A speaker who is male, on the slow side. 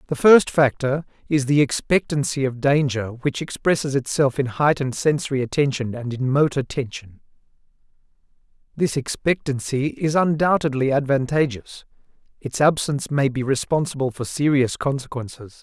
Yes: male; slow, 125 wpm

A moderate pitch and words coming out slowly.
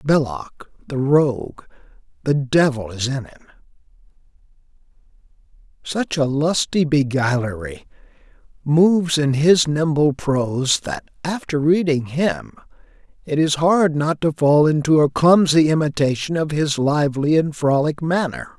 Yes: medium, 150 Hz; slow, 115 wpm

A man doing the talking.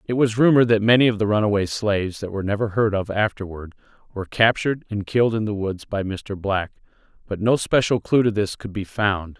Yes: male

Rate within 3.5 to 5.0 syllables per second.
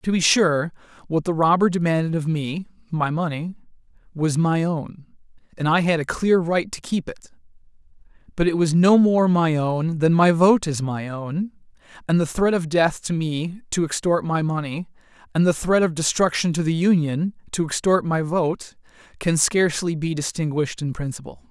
Yes: 4.8 syllables/s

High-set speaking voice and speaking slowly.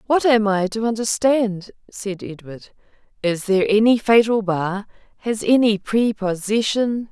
Yes: high, 215 Hz; slow, 125 wpm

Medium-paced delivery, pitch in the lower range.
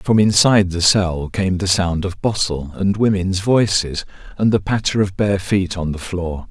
Yes: average, 195 wpm; very low, 95 Hz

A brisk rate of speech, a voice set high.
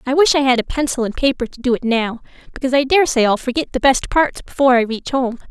Yes: fast, 260 wpm; very high, 260 Hz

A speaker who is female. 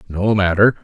No: male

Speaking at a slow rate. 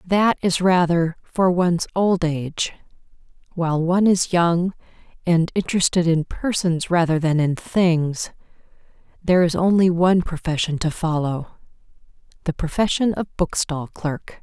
Yes: slow, 125 wpm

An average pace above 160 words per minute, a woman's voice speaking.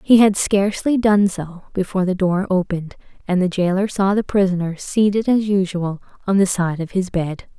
Yes: average, 190 wpm; female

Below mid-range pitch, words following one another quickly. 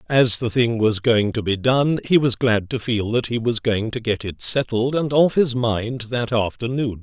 Yes: low, 120 Hz; fast, 230 wpm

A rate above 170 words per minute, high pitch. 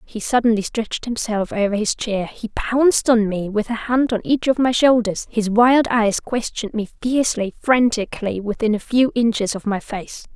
Yes: average, 190 wpm; high, 225 Hz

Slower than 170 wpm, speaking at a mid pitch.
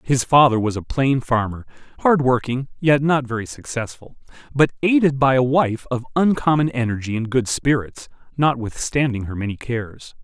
No: average, 150 wpm; low, 130 Hz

